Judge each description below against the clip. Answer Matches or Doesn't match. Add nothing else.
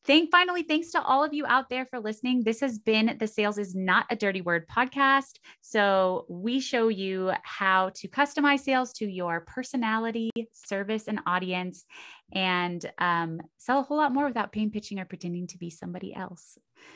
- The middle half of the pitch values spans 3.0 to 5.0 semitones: Doesn't match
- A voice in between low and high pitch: Doesn't match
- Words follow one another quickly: Doesn't match